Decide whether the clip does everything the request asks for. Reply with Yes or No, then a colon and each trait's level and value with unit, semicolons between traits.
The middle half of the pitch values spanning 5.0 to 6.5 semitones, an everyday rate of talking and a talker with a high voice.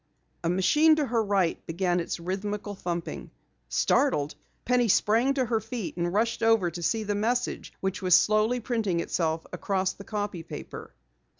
No: average, 4.4 semitones; average, 165 wpm; high, 205 Hz